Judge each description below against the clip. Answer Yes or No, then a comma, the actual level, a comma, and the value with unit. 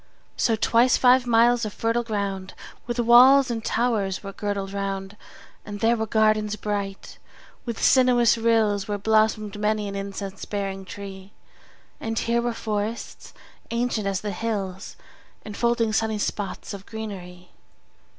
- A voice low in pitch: No, high, 215 Hz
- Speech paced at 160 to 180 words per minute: No, average, 145 wpm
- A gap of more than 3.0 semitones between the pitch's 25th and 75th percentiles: No, narrow, 2.6 semitones